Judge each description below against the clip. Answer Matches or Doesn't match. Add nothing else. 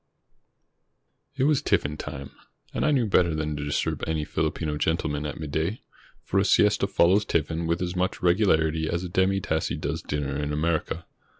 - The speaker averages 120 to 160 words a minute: Doesn't match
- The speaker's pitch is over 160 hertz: Doesn't match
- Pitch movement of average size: Matches